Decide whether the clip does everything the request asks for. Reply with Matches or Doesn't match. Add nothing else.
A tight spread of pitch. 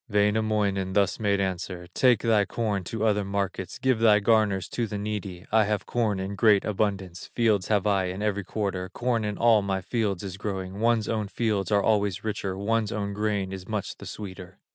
Matches